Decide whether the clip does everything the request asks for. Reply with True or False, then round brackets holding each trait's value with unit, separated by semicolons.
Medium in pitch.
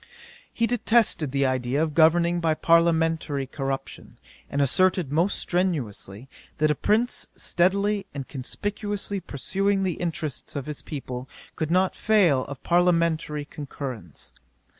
True (160 Hz)